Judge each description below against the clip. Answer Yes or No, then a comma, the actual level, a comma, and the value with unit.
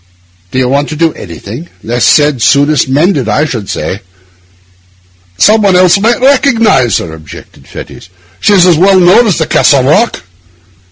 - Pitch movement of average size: No, wide, 7.6 semitones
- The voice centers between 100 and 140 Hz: No, medium, 155 Hz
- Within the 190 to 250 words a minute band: No, average, 165 wpm